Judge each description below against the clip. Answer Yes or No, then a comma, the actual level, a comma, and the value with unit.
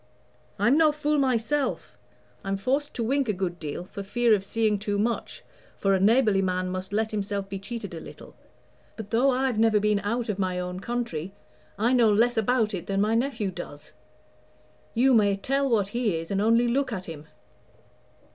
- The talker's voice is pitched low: No, high, 215 Hz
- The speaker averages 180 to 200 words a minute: Yes, average, 190 wpm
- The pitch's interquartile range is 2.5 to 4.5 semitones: Yes, average, 3.8 semitones